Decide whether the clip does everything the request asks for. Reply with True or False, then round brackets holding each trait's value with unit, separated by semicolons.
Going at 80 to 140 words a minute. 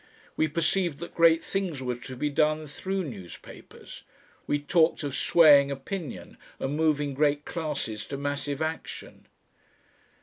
True (135 wpm)